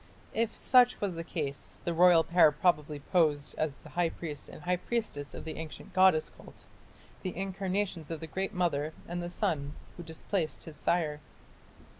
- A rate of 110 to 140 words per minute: No, average, 175 wpm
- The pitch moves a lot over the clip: No, average, 3.1 semitones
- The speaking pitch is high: No, medium, 170 Hz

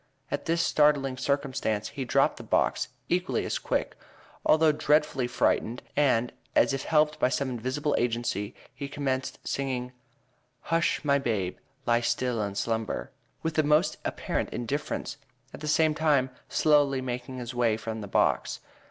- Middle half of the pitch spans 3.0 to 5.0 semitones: Yes, average, 3.7 semitones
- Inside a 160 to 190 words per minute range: No, average, 150 wpm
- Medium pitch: No, low, 130 Hz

